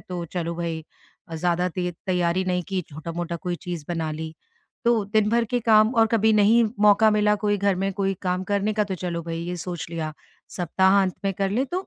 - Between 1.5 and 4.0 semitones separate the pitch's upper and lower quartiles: Yes, average, 3.4 semitones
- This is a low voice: No, medium, 185 Hz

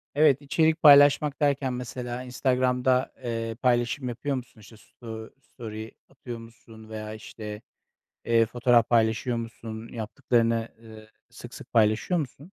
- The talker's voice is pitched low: Yes, low, 120 Hz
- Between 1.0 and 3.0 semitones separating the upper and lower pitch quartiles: Yes, narrow, 2.5 semitones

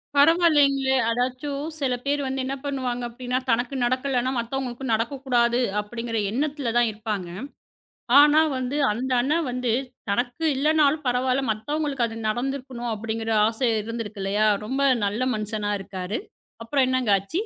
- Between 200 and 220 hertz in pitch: No, very high, 250 Hz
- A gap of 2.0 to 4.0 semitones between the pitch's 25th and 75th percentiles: Yes, average, 3.2 semitones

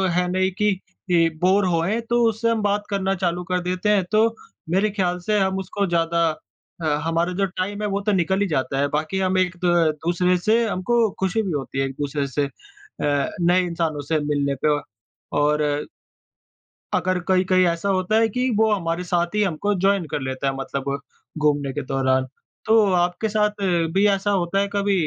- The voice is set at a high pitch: No, medium, 180 Hz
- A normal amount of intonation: Yes, average, 3.6 semitones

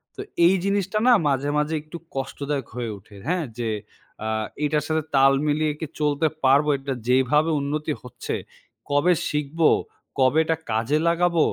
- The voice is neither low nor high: Yes, medium, 150 Hz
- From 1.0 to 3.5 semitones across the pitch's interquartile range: Yes, average, 3.0 semitones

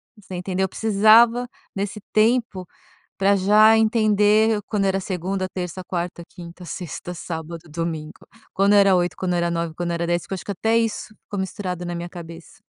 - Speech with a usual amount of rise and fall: Yes, average, 3.3 semitones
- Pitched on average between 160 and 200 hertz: Yes, high, 190 Hz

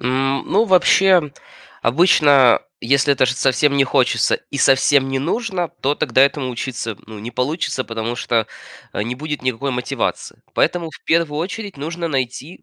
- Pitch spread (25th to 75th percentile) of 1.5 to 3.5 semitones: No, average, 4.2 semitones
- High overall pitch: No, medium, 140 Hz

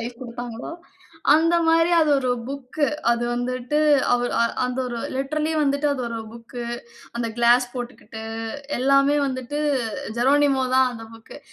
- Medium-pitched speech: No, very high, 255 Hz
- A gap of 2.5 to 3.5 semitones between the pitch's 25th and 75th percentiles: Yes, average, 2.8 semitones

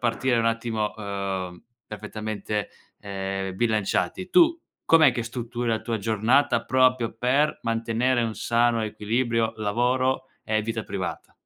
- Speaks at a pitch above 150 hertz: No, low, 115 Hz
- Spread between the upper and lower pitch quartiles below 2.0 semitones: No, narrow, 2.5 semitones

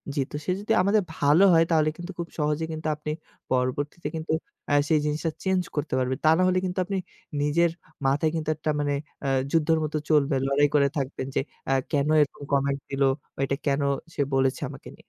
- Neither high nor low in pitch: Yes, medium, 150 Hz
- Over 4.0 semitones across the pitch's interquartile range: No, narrow, 2.6 semitones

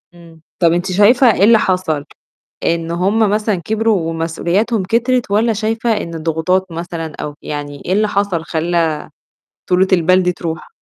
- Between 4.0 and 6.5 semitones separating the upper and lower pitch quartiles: Yes, average, 4.3 semitones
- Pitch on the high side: No, medium, 180 Hz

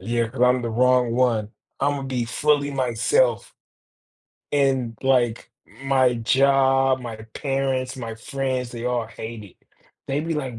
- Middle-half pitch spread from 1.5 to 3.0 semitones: Yes, narrow, 2.4 semitones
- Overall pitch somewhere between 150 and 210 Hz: No, low, 130 Hz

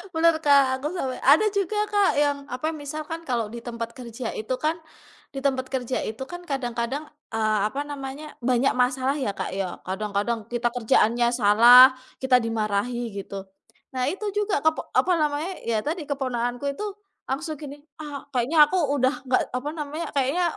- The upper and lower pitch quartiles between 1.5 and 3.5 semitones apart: No, average, 4.1 semitones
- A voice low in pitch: No, very high, 265 Hz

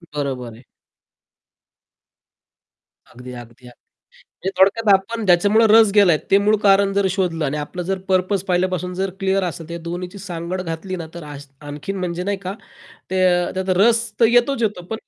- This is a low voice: No, medium, 185 Hz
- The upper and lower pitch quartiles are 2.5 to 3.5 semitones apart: Yes, average, 2.9 semitones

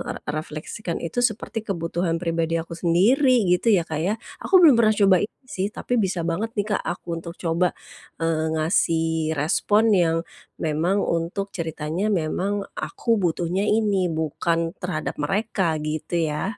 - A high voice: No, medium, 175 Hz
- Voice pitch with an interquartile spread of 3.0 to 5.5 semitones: Yes, average, 3.6 semitones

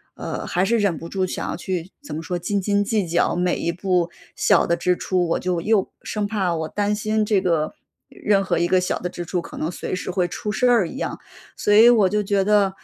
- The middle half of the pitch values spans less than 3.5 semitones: Yes, average, 2.9 semitones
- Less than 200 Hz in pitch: Yes, medium, 185 Hz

